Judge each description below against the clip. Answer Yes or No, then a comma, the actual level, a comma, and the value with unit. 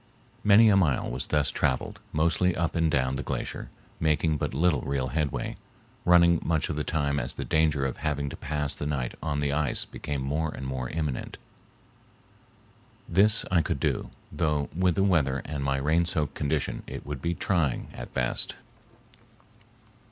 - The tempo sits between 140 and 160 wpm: No, average, 175 wpm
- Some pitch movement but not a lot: Yes, average, 3.2 semitones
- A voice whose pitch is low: Yes, very low, 75 Hz